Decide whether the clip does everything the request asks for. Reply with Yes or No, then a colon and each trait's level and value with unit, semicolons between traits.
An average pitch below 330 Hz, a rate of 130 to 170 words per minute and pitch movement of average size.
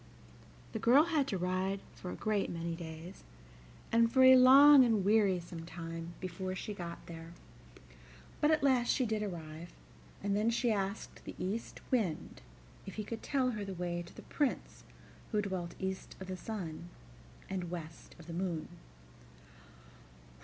Yes: high, 190 Hz; average, 160 wpm; average, 5.0 semitones